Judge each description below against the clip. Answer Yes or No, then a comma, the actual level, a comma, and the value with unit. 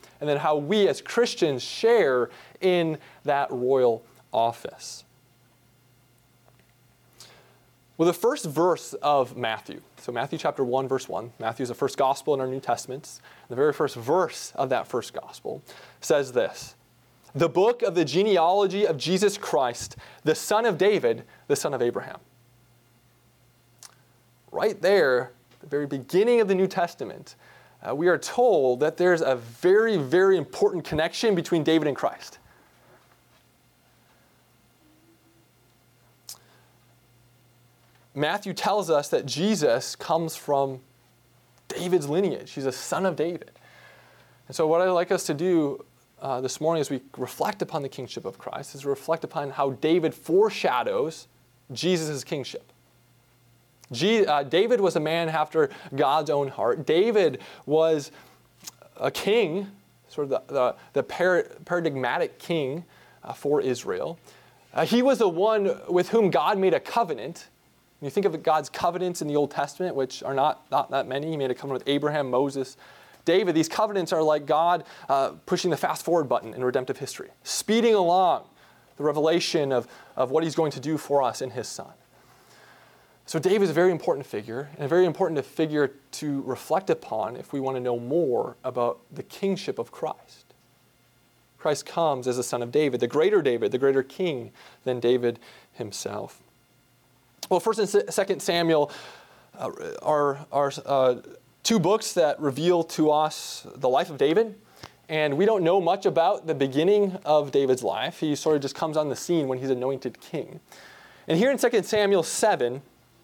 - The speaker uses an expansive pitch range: Yes, wide, 6.1 semitones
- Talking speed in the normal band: Yes, average, 160 wpm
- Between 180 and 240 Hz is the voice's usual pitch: No, medium, 150 Hz